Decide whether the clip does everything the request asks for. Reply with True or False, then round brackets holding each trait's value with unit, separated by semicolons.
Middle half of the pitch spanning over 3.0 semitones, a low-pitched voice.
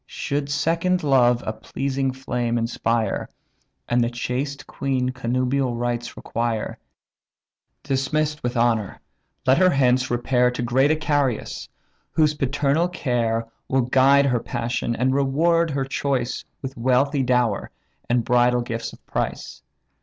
False (2.5 semitones; 130 Hz)